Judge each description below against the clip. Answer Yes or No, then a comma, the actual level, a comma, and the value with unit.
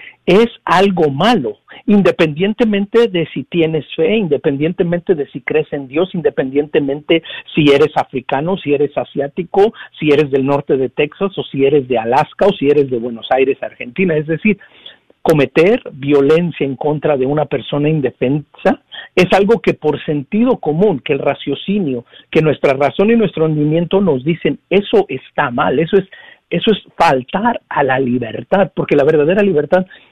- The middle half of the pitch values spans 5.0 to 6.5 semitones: Yes, wide, 5.4 semitones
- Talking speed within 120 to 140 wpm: No, average, 160 wpm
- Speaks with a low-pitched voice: No, medium, 155 Hz